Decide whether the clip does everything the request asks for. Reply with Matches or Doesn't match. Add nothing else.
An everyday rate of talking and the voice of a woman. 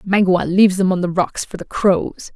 Doesn't match